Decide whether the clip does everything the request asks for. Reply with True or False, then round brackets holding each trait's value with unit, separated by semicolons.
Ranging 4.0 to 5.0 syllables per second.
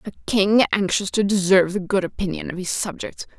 False (5.7 syllables/s)